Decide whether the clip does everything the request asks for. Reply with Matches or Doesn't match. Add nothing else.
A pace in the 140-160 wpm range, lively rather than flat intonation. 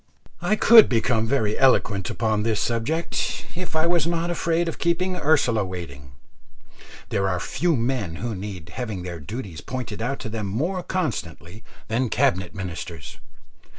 Matches